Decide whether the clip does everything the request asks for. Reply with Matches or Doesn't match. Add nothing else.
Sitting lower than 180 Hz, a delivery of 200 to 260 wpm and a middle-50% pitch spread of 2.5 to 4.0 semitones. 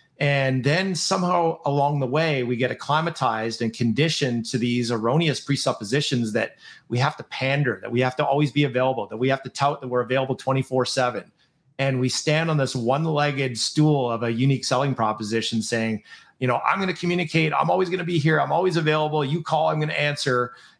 Matches